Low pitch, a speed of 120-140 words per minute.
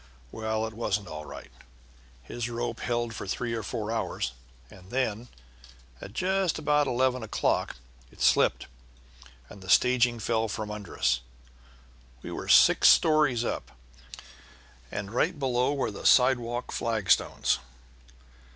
Yes: low, 115 Hz; slow, 135 wpm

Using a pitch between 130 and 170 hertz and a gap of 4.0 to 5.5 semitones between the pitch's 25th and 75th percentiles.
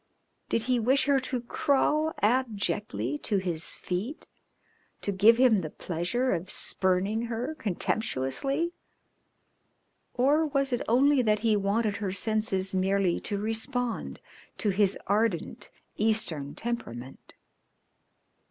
No: high, 215 Hz; average, 4.8 semitones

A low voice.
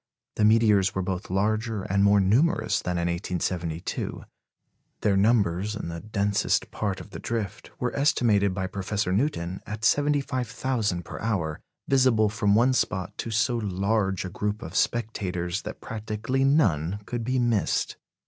Yes: low, 105 Hz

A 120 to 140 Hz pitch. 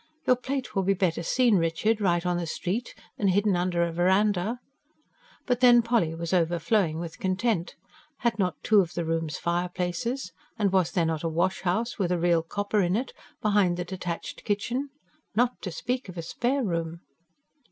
No: medium, 185 Hz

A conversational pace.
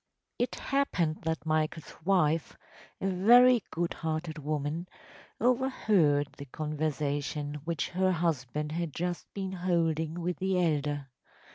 No: slow, 120 wpm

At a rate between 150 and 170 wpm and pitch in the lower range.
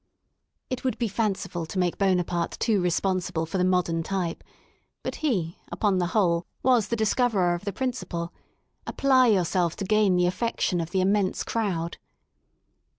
No: average, 160 wpm; medium, 185 Hz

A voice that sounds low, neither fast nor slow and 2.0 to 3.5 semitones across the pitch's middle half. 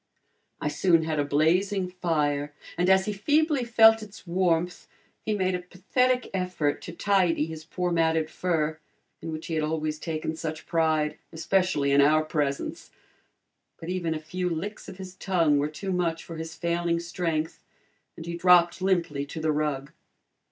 No: medium, 170 Hz; average, 170 wpm; average, 2.9 semitones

